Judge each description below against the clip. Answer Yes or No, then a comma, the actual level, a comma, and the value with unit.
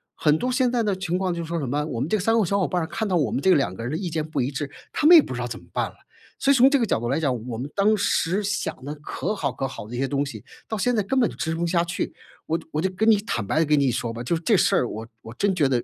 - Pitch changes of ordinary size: No, wide, 7.1 semitones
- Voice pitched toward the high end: No, medium, 165 Hz